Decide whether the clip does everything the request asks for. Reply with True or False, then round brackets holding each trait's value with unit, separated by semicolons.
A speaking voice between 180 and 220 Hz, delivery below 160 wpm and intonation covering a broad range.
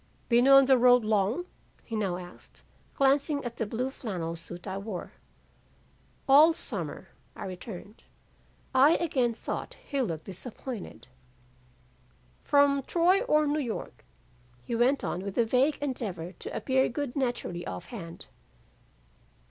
False (245 Hz; 135 wpm; 6.0 semitones)